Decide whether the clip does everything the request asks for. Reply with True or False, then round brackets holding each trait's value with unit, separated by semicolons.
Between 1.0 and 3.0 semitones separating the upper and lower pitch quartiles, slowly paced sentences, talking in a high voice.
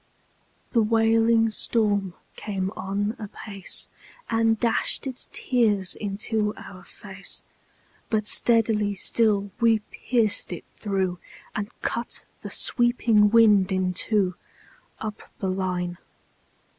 True (2.6 semitones; 105 wpm; 210 Hz)